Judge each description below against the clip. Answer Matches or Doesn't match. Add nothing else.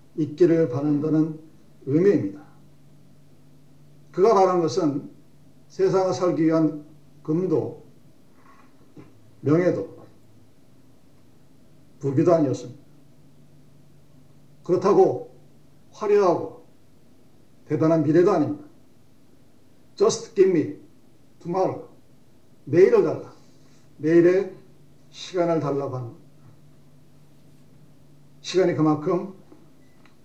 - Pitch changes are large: Doesn't match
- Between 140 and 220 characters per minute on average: Matches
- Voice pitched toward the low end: Doesn't match